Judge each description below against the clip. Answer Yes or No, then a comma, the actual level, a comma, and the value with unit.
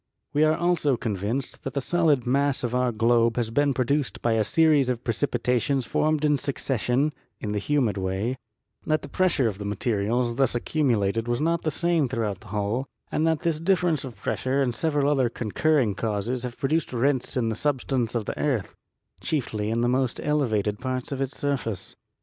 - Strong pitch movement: No, average, 4.2 semitones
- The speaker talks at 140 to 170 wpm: No, average, 190 wpm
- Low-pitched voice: Yes, low, 125 Hz